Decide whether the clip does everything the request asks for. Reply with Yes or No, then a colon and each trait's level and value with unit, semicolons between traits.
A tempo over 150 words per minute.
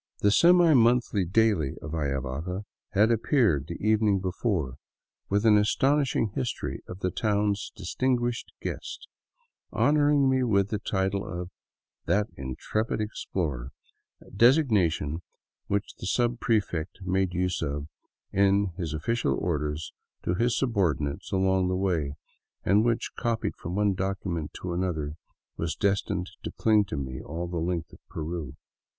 No: average, 140 wpm